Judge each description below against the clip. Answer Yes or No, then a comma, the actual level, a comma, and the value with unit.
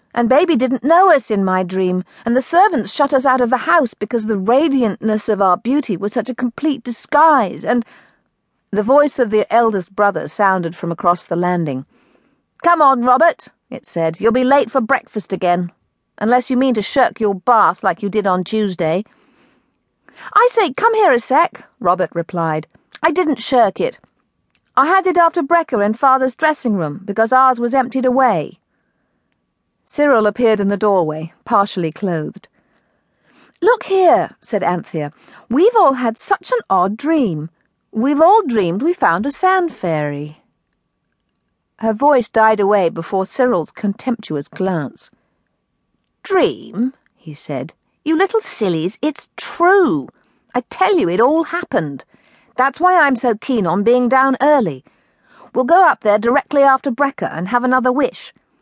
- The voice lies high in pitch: Yes, high, 245 Hz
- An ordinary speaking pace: Yes, average, 160 wpm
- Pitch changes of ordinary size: No, wide, 6.9 semitones